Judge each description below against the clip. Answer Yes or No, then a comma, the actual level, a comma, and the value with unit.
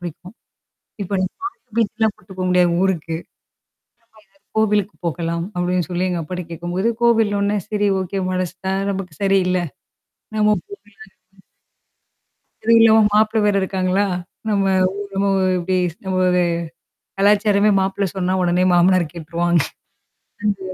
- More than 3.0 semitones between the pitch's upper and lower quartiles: No, narrow, 2.4 semitones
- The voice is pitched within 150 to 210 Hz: Yes, high, 190 Hz